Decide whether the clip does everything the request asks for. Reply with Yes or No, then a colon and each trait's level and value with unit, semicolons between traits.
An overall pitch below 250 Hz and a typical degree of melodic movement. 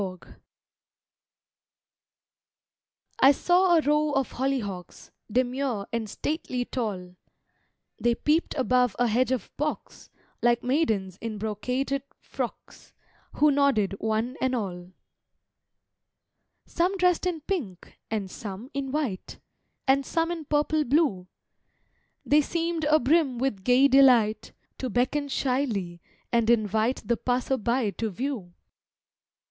No: very high, 255 Hz; average, 4.9 semitones